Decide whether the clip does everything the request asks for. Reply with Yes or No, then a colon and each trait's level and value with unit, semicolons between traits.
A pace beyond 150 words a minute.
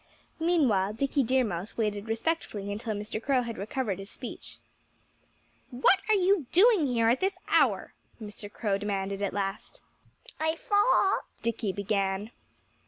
No: average, 145 wpm